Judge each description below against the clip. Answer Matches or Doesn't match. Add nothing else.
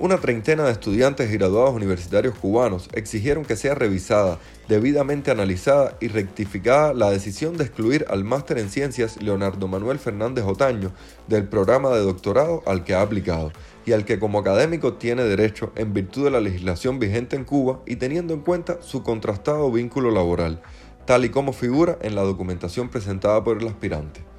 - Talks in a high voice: Doesn't match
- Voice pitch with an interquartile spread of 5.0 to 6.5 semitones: Matches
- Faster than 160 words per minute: Matches